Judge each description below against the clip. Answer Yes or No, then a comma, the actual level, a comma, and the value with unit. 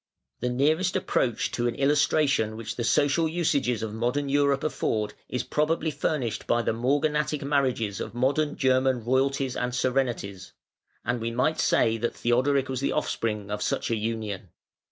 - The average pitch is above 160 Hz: No, low, 130 Hz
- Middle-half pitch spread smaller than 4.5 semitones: Yes, average, 3.8 semitones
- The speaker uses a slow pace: No, average, 160 wpm